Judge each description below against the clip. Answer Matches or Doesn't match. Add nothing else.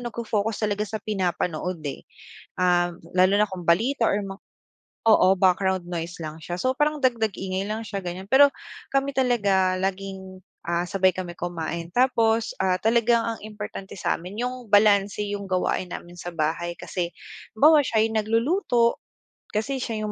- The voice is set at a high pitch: Matches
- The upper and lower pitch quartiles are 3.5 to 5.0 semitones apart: Matches